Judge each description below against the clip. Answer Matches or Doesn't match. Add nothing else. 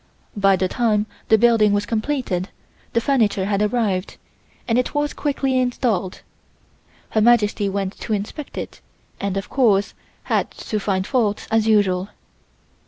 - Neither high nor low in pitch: Doesn't match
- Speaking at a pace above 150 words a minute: Doesn't match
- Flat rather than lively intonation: Doesn't match